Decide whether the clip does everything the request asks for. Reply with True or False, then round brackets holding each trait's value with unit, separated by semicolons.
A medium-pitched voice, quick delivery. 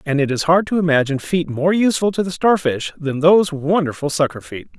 True (160 Hz; 215 wpm)